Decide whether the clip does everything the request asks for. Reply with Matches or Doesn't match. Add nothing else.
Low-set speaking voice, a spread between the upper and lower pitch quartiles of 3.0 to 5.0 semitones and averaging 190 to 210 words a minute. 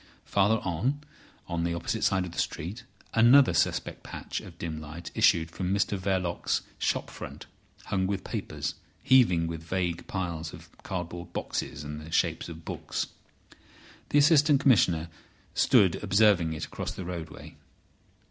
Doesn't match